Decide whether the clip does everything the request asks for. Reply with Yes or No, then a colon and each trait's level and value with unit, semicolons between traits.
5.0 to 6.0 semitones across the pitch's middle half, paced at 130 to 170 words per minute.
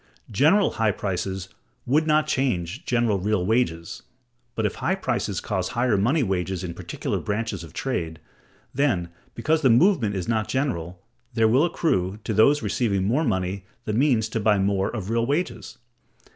Yes: wide, 5.6 semitones; average, 165 wpm